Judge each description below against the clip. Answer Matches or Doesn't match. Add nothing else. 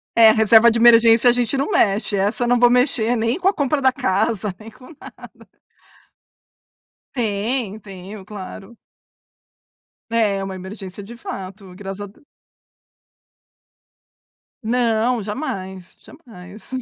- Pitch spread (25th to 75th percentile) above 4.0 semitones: Doesn't match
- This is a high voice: Matches